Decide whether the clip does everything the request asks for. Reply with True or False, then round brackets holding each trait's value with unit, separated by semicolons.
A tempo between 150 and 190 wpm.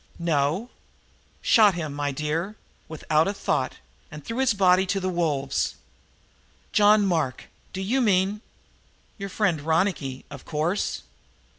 False (135 wpm)